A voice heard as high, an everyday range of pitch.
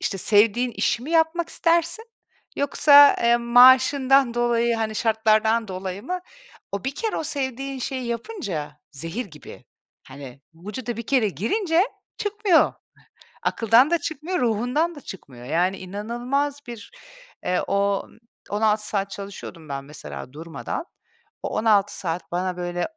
No: high, 230 Hz; wide, 6.2 semitones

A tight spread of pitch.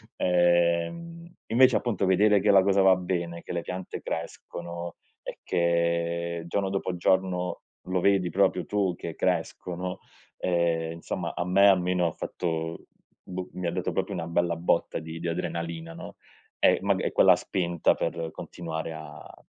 Yes: narrow, 1.8 semitones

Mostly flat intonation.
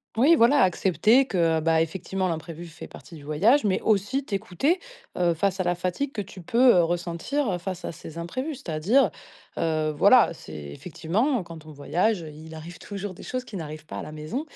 No: wide, 5.6 semitones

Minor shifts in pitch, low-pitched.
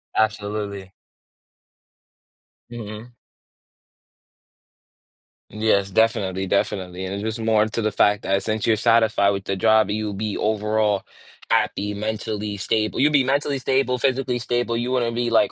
Yes: narrow, 2.3 semitones; low, 110 Hz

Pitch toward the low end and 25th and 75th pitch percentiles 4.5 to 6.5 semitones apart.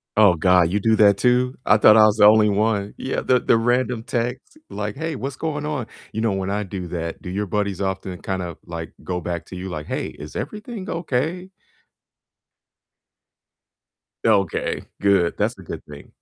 Yes: low, 105 Hz; average, 5.1 semitones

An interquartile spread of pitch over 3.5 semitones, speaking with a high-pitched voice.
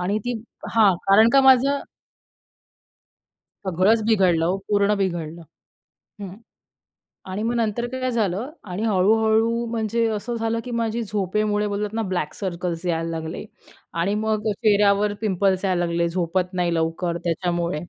Yes: average, 3.9 semitones; high, 200 Hz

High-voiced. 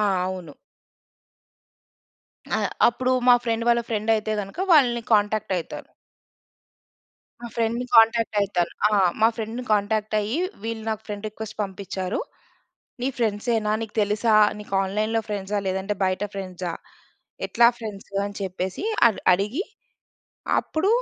Yes: high, 215 Hz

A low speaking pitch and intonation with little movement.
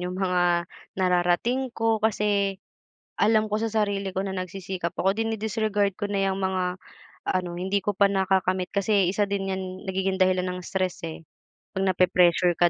No: high, 190 Hz; narrow, 2.0 semitones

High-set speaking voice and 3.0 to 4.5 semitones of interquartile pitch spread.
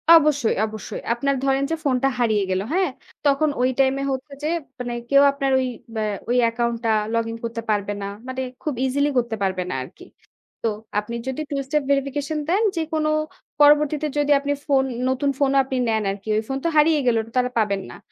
Yes: very high, 265 Hz; average, 4.1 semitones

